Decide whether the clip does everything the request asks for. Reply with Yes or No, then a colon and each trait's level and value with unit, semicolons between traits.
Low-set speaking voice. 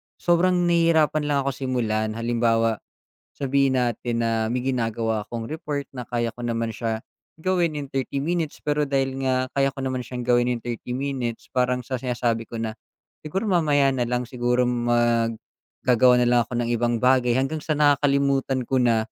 Yes: low, 125 Hz